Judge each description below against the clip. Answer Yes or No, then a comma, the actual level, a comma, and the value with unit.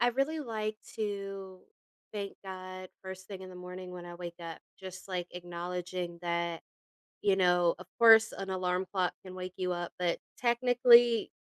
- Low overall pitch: No, medium, 185 Hz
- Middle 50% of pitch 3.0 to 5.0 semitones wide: No, narrow, 2.6 semitones